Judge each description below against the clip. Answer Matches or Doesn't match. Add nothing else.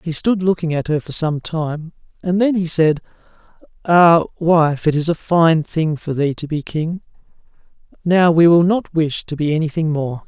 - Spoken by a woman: Doesn't match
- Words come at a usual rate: Matches